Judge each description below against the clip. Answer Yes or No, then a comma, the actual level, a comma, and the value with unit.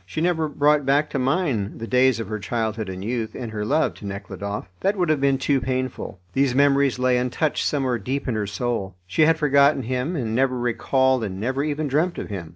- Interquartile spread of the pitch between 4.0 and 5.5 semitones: Yes, average, 4.4 semitones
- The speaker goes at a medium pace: No, fast, 220 wpm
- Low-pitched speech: Yes, low, 130 Hz